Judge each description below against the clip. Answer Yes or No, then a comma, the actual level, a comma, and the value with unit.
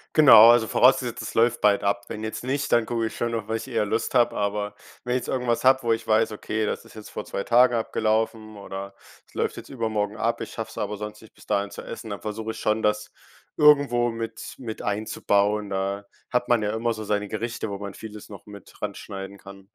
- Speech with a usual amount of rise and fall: No, narrow, 2.2 semitones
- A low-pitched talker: Yes, low, 110 Hz